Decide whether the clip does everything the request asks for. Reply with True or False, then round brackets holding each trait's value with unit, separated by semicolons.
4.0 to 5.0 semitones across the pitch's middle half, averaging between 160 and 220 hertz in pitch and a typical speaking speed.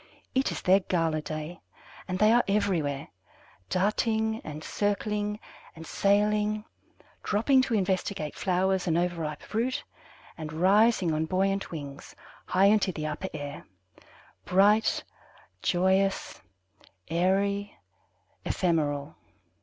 False (4.3 semitones; 190 Hz; 105 wpm)